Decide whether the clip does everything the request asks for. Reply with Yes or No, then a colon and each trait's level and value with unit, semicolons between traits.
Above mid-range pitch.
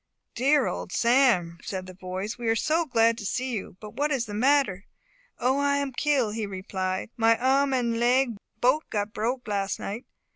Yes: high, 235 Hz